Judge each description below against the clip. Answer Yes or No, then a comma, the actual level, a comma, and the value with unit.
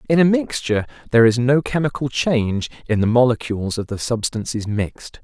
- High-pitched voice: No, low, 125 Hz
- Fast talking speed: No, average, 170 wpm